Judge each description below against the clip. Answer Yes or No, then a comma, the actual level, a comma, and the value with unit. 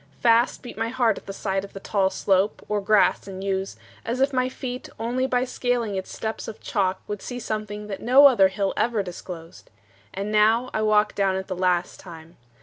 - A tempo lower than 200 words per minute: No, fast, 205 wpm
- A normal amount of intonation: Yes, average, 3.7 semitones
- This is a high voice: Yes, high, 210 Hz